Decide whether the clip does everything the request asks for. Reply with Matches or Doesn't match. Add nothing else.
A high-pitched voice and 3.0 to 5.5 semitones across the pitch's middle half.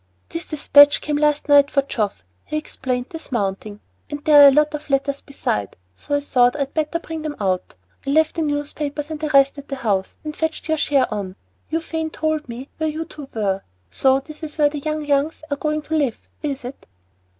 Doesn't match